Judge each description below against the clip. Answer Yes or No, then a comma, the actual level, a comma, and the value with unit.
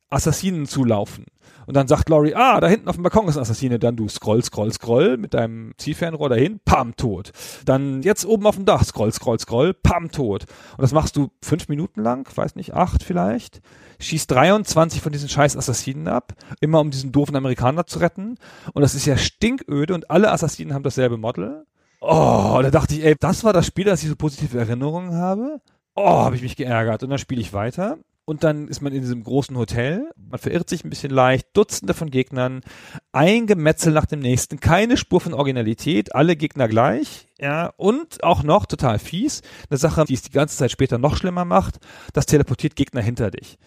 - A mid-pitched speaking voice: Yes, medium, 145 Hz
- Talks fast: Yes, fast, 205 wpm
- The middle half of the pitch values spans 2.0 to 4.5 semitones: No, average, 5.1 semitones